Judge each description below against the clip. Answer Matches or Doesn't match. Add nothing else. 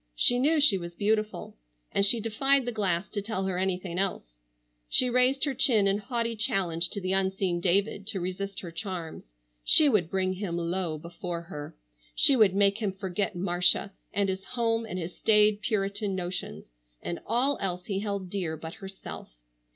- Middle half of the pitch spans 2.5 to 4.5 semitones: Matches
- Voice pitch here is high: Matches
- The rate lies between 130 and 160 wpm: Doesn't match